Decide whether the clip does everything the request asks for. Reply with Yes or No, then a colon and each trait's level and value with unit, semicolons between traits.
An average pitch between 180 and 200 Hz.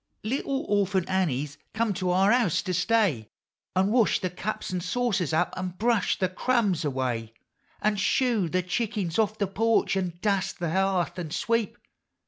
Yes: high, 190 Hz